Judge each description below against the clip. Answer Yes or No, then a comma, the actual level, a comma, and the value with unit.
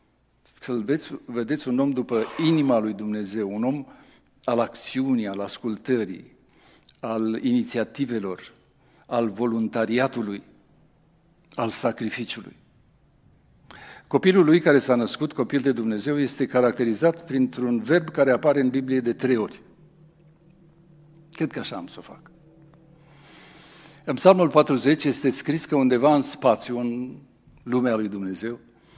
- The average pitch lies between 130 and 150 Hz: Yes, low, 135 Hz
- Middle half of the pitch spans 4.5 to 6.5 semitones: Yes, average, 5.1 semitones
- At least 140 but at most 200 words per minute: No, average, 125 wpm